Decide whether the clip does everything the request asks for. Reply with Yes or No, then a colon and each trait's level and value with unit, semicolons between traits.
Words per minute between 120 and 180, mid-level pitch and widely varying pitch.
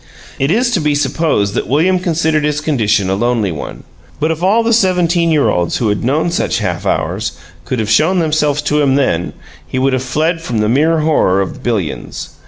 No: average, 200 wpm; medium, 150 Hz; wide, 5.9 semitones